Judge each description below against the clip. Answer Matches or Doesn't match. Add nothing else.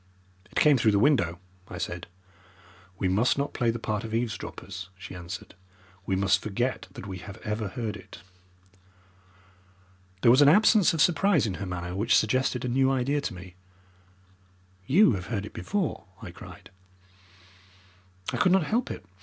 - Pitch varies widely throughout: Matches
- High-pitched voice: Doesn't match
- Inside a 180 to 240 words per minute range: Doesn't match